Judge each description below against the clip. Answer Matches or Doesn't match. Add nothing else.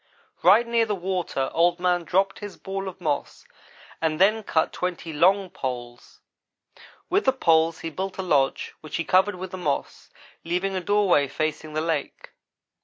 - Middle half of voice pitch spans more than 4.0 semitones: Doesn't match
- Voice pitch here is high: Doesn't match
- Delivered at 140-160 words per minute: Doesn't match